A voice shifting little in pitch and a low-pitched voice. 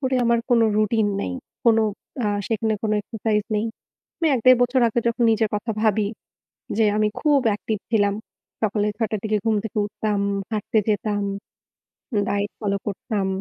No: narrow, 1.7 semitones; high, 215 Hz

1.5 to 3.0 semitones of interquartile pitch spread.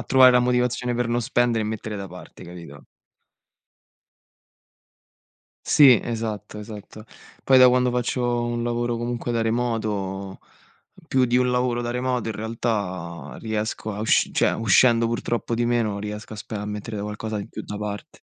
Yes: narrow, 2.5 semitones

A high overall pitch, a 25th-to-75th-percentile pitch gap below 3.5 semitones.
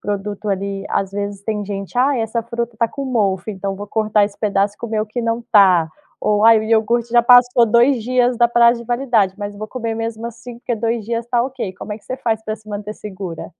Yes: high, 220 Hz; narrow, 2.6 semitones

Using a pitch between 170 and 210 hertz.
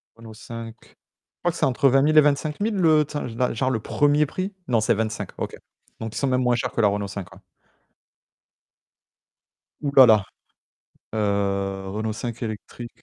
No: low, 115 Hz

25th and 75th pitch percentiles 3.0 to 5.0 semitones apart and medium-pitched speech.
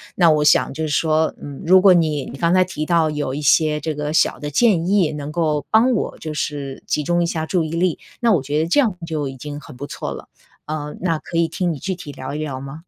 No: narrow, 2.6 semitones; medium, 155 Hz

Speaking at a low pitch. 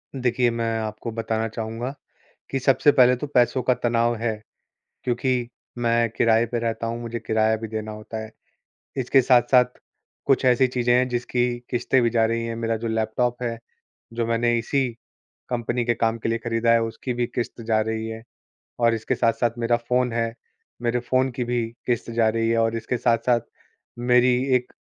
Yes: low, 120 Hz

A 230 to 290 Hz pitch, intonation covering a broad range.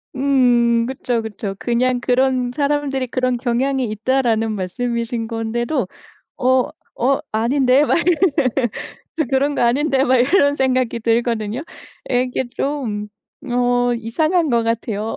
No: high, 245 Hz; narrow, 2.5 semitones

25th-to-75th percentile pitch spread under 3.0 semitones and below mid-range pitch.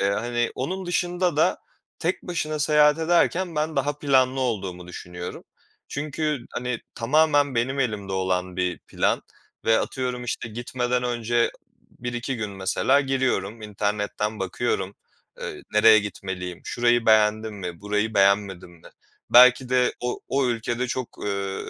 No: average, 4.8 semitones; low, 120 Hz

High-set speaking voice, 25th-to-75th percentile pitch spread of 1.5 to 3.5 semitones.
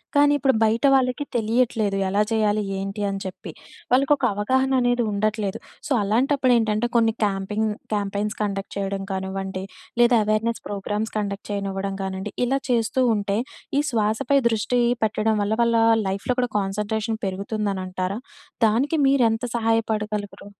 Yes: high, 215 Hz; average, 3.0 semitones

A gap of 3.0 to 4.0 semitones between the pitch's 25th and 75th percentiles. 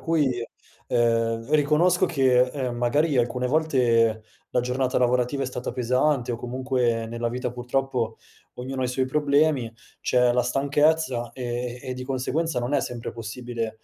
No: narrow, 2.4 semitones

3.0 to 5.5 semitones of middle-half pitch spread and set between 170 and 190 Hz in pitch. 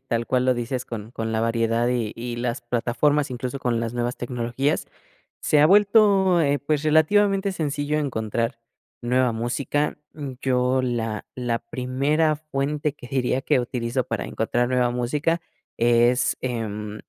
No: average, 3.7 semitones; low, 125 Hz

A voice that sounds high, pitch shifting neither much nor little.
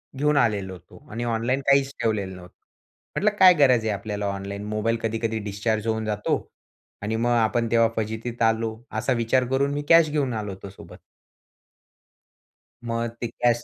No: low, 115 Hz; average, 3.0 semitones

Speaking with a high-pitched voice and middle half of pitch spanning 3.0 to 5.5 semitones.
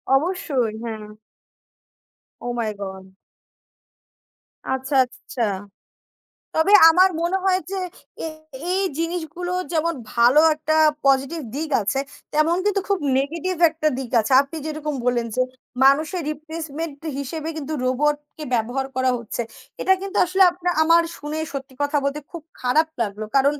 Yes: very high, 300 Hz; average, 4.1 semitones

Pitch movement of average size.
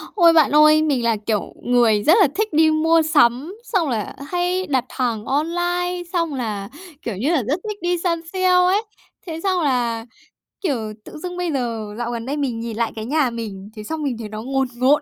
No: wide, 6.6 semitones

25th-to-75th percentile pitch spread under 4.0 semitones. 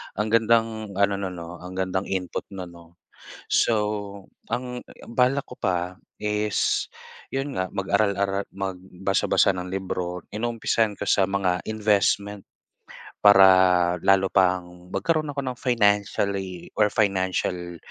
Yes: narrow, 2.5 semitones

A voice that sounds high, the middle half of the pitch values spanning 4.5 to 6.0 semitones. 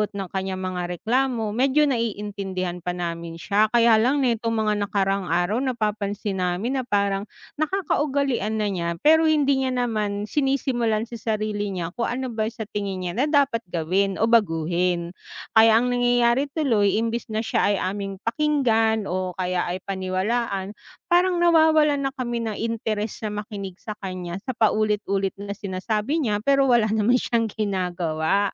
No: high, 215 Hz; average, 4.0 semitones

